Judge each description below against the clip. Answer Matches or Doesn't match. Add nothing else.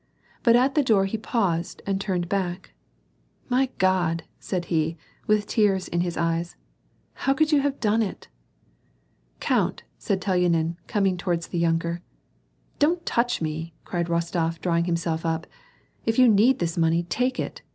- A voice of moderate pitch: Matches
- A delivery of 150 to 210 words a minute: Matches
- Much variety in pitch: Doesn't match